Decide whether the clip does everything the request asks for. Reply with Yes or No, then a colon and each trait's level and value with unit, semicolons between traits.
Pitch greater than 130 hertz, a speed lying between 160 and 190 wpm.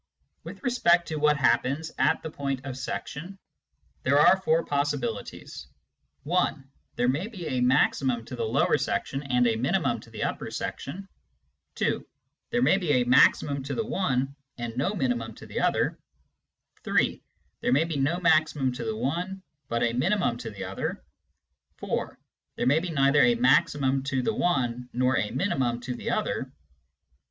Yes: medium, 140 Hz; average, 170 wpm